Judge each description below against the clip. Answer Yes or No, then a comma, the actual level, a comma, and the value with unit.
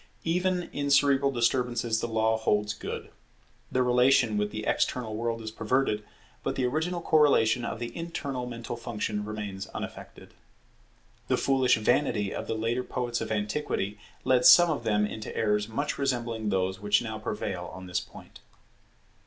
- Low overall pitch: Yes, low, 115 Hz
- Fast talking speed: No, average, 160 wpm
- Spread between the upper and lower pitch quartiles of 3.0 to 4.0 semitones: Yes, average, 3.5 semitones